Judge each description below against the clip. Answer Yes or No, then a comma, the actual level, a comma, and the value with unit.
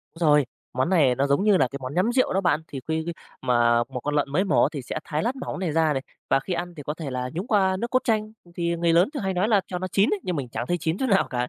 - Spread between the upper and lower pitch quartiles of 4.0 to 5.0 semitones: No, wide, 5.5 semitones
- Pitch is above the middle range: No, medium, 170 Hz